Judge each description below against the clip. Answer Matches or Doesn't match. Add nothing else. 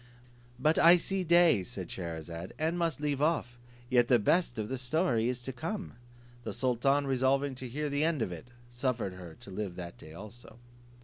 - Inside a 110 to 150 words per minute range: Doesn't match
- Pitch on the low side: Matches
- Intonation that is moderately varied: Doesn't match